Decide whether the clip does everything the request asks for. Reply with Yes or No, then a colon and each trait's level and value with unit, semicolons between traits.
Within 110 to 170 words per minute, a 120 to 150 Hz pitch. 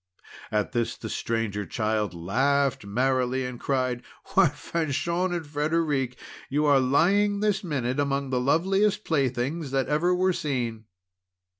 Yes: slow, 135 wpm; medium, 140 Hz